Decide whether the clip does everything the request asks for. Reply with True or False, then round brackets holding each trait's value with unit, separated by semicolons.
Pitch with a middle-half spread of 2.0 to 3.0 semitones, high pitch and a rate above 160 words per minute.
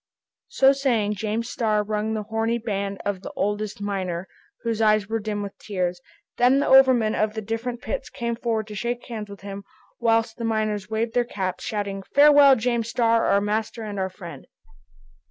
True (2.5 semitones; 220 Hz; 185 wpm)